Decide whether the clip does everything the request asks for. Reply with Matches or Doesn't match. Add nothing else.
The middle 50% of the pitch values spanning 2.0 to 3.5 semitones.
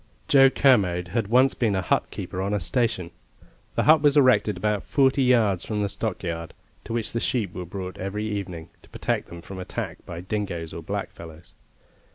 Doesn't match